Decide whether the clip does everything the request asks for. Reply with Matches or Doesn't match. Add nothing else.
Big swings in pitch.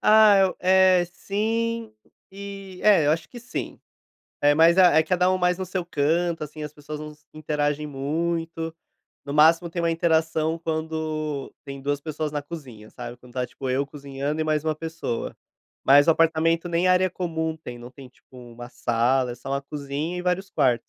Doesn't match